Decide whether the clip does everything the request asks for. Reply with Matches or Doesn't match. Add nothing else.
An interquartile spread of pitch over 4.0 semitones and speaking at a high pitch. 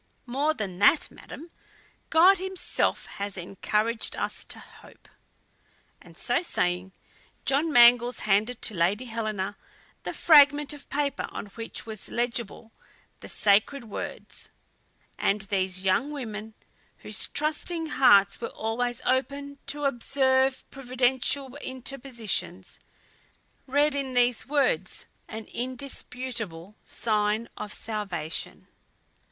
Matches